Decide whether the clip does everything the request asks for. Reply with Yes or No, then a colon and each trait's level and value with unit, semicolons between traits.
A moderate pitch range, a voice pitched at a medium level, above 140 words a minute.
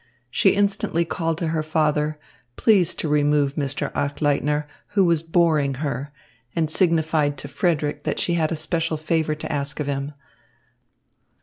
No: narrow, 2.2 semitones; medium, 155 Hz; average, 150 wpm